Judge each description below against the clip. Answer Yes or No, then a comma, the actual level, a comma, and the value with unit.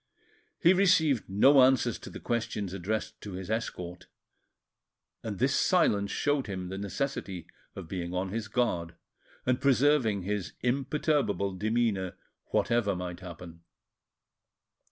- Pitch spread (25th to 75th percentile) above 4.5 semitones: Yes, wide, 5.4 semitones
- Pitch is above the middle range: No, low, 105 Hz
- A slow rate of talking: Yes, slow, 125 wpm